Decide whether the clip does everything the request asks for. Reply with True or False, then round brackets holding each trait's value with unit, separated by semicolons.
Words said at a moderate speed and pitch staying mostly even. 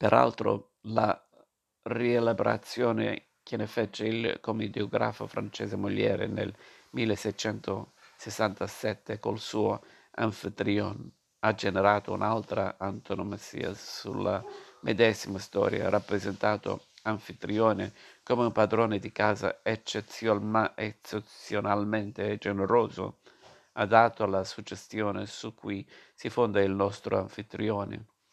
False (85 wpm; 1.8 semitones)